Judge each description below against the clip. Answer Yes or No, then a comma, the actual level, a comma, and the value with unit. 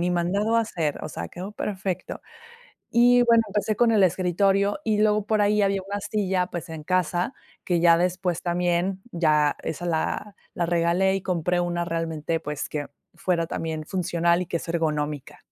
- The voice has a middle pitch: Yes, medium, 180 Hz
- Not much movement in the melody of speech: No, average, 3.0 semitones